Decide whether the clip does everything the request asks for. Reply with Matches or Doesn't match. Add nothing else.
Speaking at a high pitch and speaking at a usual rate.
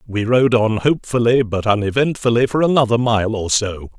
Doesn't match